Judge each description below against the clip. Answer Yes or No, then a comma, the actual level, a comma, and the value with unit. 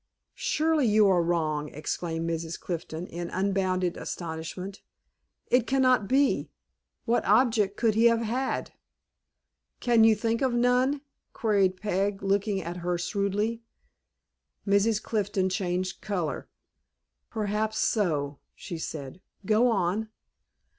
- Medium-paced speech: No, slow, 115 wpm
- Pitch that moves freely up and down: No, average, 4.3 semitones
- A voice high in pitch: Yes, high, 200 Hz